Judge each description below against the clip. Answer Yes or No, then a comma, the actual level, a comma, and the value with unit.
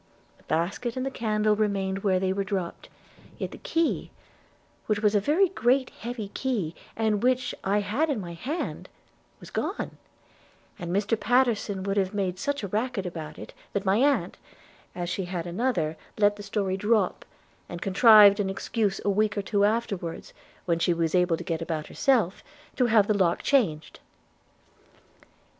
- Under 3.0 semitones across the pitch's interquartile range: No, average, 3.8 semitones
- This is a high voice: Yes, high, 205 Hz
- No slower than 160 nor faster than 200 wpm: Yes, average, 170 wpm